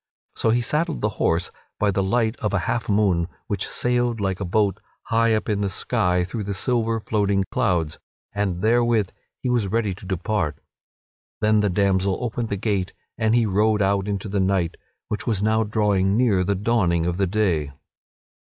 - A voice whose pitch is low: Yes, low, 105 Hz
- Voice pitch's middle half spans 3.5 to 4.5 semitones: No, average, 2.8 semitones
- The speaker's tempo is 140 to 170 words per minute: No, average, 185 wpm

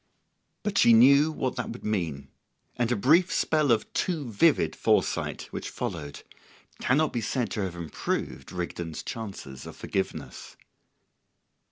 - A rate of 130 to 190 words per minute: Yes, average, 140 wpm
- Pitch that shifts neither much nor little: No, wide, 8.4 semitones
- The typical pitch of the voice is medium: No, low, 115 Hz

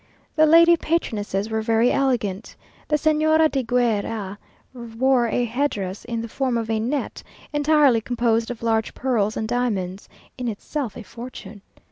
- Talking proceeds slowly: No, average, 160 wpm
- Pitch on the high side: Yes, high, 235 Hz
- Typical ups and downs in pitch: Yes, average, 3.6 semitones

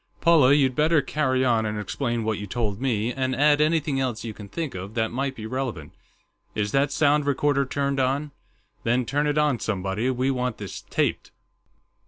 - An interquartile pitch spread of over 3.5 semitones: Yes, average, 4.3 semitones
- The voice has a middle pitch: No, low, 130 Hz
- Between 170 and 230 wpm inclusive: Yes, average, 190 wpm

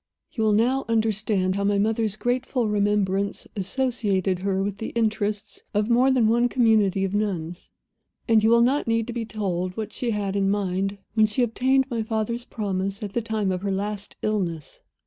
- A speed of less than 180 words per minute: No, average, 185 wpm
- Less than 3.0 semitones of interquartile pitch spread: Yes, narrow, 2.6 semitones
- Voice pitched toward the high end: Yes, high, 210 Hz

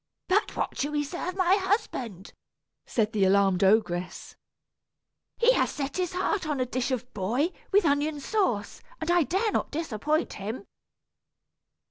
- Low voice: No, very high, 290 Hz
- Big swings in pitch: Yes, wide, 8.9 semitones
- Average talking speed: Yes, average, 150 wpm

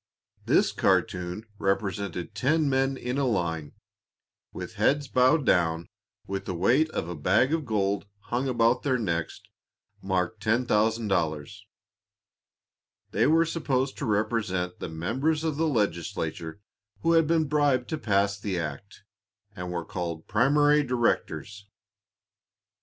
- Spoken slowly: Yes, slow, 130 wpm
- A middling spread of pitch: No, wide, 7.1 semitones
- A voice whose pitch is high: No, low, 105 Hz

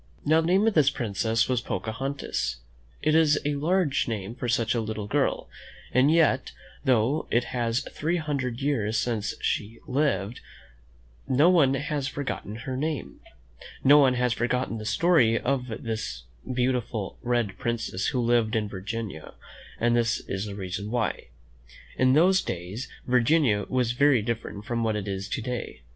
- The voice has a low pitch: Yes, low, 120 Hz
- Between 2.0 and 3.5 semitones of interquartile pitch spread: No, average, 4.2 semitones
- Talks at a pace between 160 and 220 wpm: Yes, average, 165 wpm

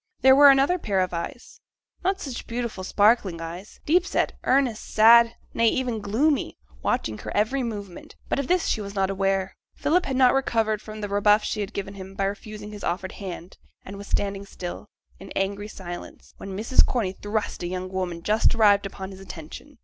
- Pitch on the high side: Yes, high, 205 Hz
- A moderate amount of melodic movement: Yes, average, 3.6 semitones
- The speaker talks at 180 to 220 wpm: Yes, average, 195 wpm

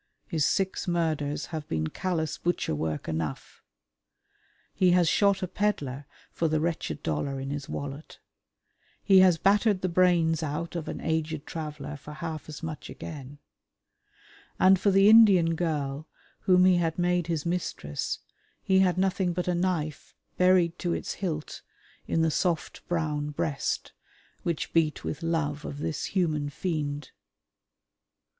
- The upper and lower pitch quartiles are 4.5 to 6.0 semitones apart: No, average, 3.4 semitones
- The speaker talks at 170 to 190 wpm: No, average, 150 wpm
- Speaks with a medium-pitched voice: Yes, medium, 165 Hz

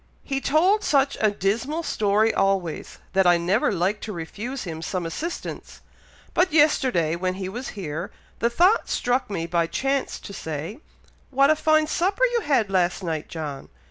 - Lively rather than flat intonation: Yes, wide, 8.0 semitones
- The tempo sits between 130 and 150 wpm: No, average, 170 wpm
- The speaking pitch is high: Yes, high, 210 Hz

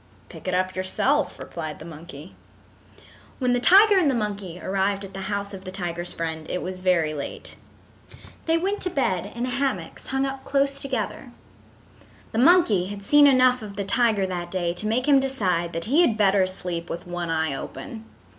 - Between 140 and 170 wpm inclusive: No, average, 190 wpm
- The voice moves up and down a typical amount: No, wide, 6.7 semitones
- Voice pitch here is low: No, high, 200 Hz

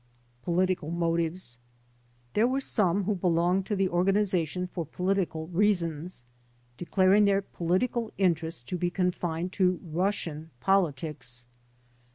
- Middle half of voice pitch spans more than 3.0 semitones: No, average, 2.7 semitones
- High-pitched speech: No, medium, 180 Hz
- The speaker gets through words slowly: Yes, slow, 110 wpm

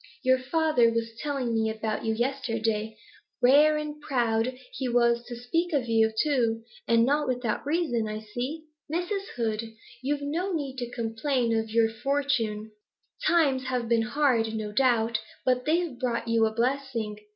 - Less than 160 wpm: No, average, 165 wpm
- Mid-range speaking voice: No, high, 245 Hz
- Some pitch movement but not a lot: Yes, average, 4.0 semitones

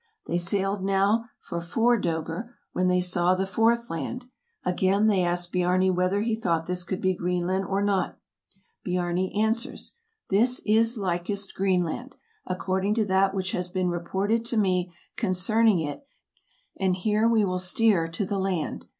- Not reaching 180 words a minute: Yes, average, 160 wpm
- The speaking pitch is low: No, high, 190 Hz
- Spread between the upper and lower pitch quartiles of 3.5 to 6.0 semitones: No, average, 2.9 semitones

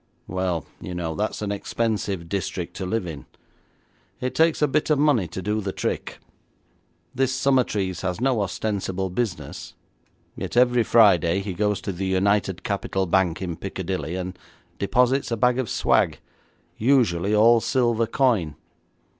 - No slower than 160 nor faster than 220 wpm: No, average, 150 wpm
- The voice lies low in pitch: Yes, low, 100 Hz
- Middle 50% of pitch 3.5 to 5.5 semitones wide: Yes, average, 4.4 semitones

